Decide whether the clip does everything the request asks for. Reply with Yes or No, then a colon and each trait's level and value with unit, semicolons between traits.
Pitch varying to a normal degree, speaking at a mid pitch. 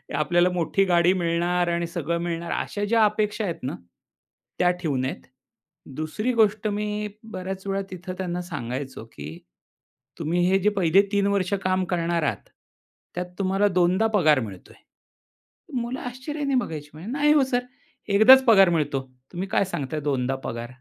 Yes: average, 4.0 semitones; medium, 180 Hz